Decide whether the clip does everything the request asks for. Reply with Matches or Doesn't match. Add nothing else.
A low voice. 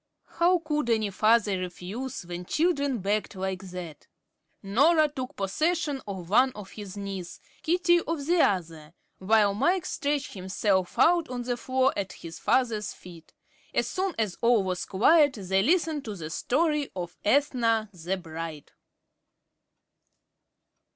Doesn't match